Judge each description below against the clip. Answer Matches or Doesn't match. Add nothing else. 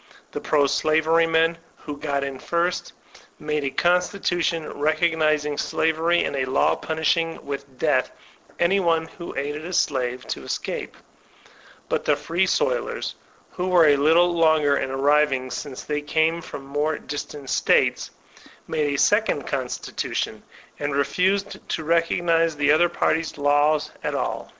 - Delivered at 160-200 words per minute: Doesn't match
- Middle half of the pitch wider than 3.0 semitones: Doesn't match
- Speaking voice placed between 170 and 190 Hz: Doesn't match